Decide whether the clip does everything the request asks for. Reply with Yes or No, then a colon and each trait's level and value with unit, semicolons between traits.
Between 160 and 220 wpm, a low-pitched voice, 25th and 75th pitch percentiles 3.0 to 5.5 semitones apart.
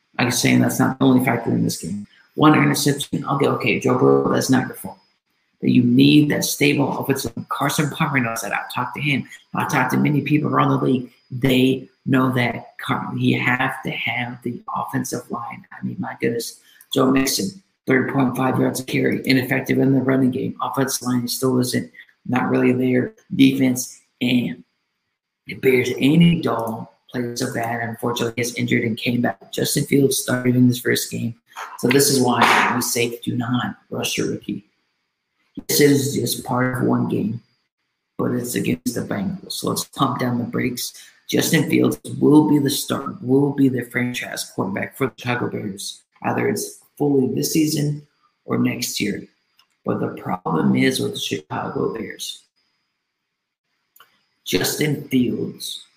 No: average, 175 wpm; low, 125 Hz; narrow, 2.5 semitones